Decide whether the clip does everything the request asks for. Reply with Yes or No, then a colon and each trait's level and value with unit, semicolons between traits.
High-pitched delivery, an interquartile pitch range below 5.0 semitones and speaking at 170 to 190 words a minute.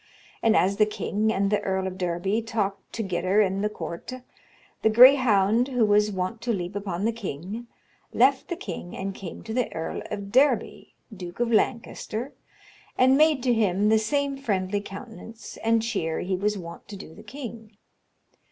Yes: high, 210 Hz; average, 3.4 semitones; average, 175 wpm